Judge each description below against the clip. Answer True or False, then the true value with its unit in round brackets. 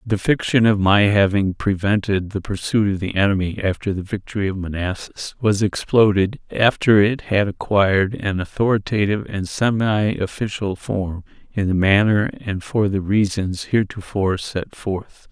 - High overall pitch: False (100 Hz)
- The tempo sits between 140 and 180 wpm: True (150 wpm)